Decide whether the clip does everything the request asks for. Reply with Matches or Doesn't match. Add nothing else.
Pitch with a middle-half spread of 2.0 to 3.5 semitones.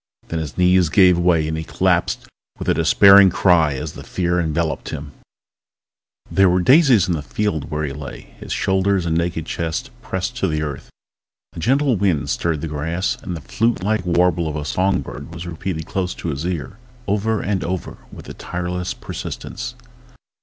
Matches